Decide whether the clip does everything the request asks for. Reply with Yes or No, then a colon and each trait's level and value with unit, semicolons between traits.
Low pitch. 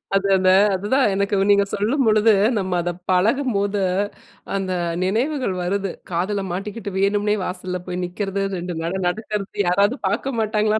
No: high, 200 Hz